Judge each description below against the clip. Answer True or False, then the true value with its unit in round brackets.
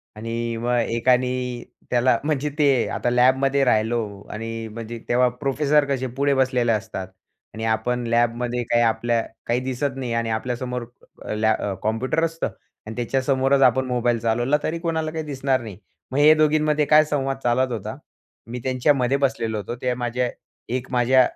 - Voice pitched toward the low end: True (125 Hz)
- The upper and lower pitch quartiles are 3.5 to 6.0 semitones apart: False (2.6 semitones)